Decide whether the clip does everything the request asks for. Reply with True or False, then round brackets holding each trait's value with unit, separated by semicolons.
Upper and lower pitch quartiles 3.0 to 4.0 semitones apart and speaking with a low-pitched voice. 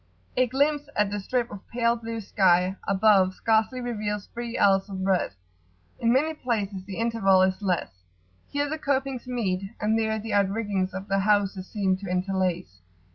False (3.6 semitones; 205 Hz)